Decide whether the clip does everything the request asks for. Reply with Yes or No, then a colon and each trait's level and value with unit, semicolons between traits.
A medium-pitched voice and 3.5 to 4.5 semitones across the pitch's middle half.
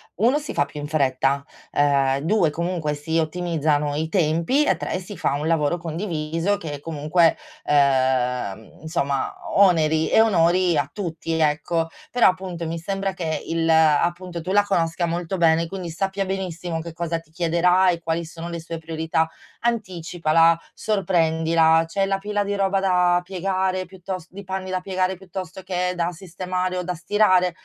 No: medium, 170 Hz; narrow, 2.6 semitones